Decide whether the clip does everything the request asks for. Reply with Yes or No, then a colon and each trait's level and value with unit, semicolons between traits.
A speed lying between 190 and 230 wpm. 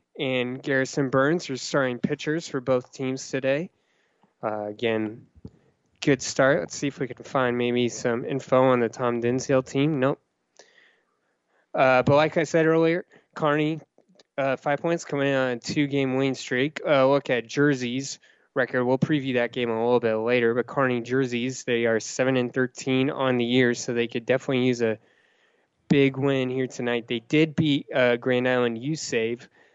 No: average, 180 wpm